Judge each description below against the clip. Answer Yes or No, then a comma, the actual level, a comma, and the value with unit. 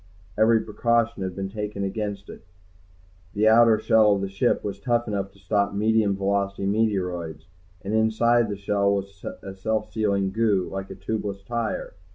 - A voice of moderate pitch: No, low, 100 Hz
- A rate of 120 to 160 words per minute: No, average, 170 wpm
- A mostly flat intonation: Yes, narrow, 2.0 semitones